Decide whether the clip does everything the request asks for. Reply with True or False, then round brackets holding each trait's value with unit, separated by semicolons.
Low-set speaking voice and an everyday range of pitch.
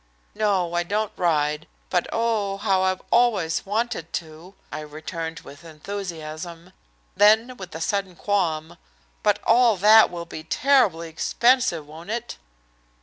False (185 Hz; 4.6 semitones)